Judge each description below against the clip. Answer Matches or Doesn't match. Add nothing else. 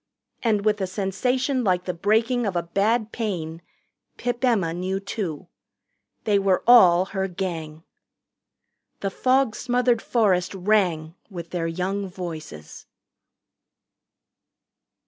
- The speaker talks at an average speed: Doesn't match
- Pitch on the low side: Doesn't match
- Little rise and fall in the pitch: Doesn't match